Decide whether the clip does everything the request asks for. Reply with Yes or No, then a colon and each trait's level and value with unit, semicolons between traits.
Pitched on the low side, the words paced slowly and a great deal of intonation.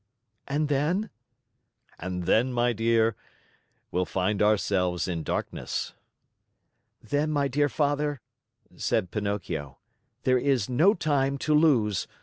Yes: low, 120 Hz; slow, 115 wpm; wide, 6.4 semitones